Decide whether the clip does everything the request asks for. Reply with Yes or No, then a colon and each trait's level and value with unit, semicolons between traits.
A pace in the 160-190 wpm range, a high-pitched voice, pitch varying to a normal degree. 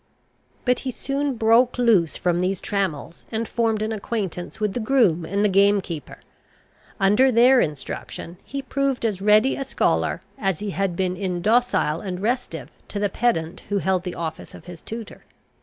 Yes: average, 175 wpm; high, 205 Hz; average, 4.6 semitones